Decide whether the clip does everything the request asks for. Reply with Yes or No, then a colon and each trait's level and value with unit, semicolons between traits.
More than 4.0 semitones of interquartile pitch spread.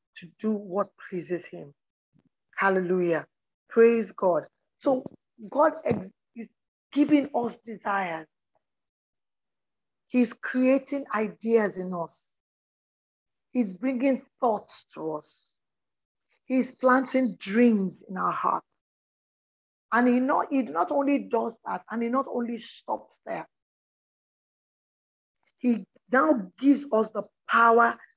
Yes: average, 4.4 semitones